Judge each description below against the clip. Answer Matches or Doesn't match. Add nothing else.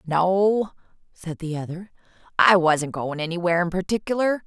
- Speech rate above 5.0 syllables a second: Doesn't match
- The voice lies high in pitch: Doesn't match